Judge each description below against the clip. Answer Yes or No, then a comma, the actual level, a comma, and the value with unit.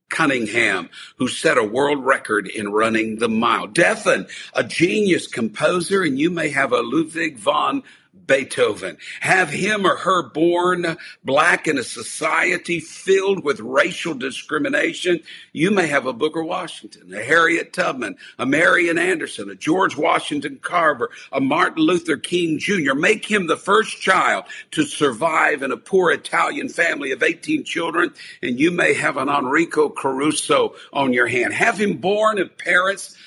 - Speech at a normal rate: Yes, average, 155 wpm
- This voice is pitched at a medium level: No, high, 215 Hz